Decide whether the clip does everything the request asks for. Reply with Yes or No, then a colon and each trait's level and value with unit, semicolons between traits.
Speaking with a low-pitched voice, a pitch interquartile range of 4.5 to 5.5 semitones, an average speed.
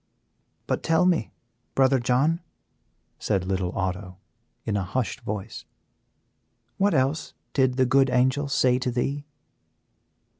No: low, 130 Hz; average, 4.9 semitones; slow, 120 wpm